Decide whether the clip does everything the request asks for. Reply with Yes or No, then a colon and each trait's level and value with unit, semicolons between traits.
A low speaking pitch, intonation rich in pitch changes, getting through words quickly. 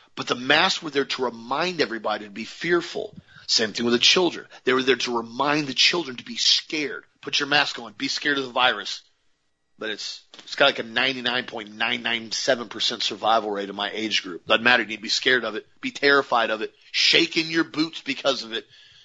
Yes: low, 130 Hz; wide, 7.3 semitones; fast, 215 wpm